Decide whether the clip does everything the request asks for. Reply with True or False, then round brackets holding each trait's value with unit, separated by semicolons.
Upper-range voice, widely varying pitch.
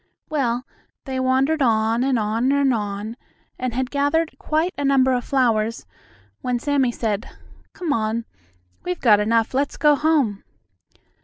False (255 Hz; 3.8 semitones)